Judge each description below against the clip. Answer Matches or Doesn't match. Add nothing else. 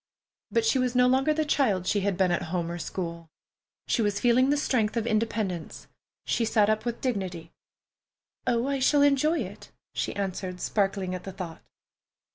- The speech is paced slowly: Doesn't match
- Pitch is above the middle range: Matches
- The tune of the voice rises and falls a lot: Matches